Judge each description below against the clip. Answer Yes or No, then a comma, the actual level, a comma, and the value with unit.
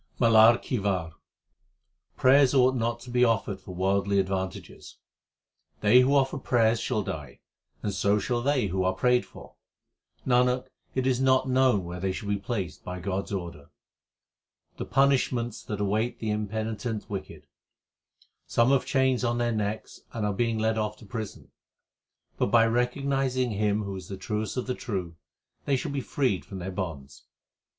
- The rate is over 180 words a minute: No, average, 170 wpm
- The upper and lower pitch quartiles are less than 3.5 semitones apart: No, average, 4.2 semitones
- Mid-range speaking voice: No, low, 110 Hz